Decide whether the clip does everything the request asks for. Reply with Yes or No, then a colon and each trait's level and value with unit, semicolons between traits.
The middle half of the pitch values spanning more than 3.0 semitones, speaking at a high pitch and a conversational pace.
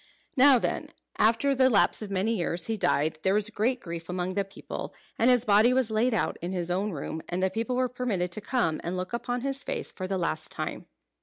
No: average, 5.3 semitones; high, 210 Hz; fast, 230 wpm